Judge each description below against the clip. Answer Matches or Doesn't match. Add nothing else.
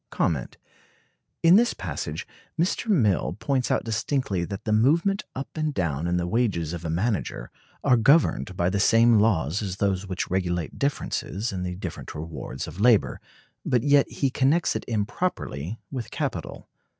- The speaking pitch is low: Matches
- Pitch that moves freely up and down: Matches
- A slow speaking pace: Doesn't match